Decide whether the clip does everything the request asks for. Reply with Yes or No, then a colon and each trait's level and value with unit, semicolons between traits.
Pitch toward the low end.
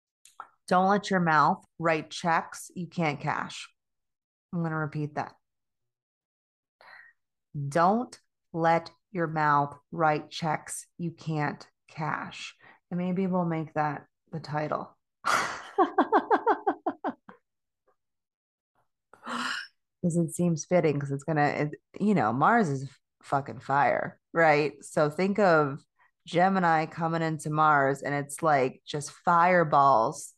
No: medium, 160 Hz